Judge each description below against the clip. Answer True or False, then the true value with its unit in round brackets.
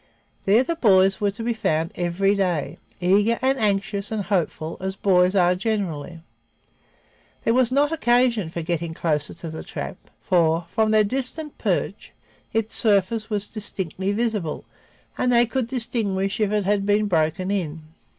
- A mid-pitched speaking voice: False (200 Hz)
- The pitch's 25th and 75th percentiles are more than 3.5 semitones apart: True (4.0 semitones)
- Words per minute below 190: True (160 wpm)